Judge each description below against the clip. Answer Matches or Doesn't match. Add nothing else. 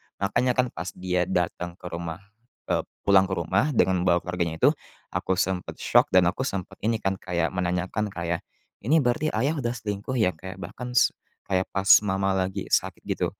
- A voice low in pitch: Matches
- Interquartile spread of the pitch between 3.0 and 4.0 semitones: Matches